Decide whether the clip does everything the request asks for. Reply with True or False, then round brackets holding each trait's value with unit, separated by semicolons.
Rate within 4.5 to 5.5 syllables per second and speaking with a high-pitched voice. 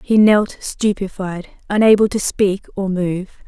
False (4.2 syllables/s; 200 Hz)